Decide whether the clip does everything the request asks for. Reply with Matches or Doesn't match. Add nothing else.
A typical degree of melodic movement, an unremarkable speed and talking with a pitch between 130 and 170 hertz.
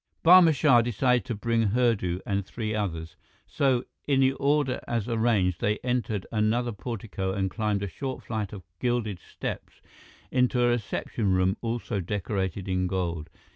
Doesn't match